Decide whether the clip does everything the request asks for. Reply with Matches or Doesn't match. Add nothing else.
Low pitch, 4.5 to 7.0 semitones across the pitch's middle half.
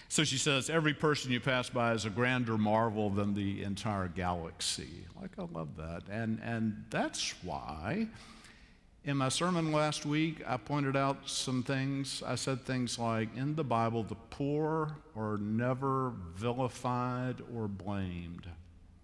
Matches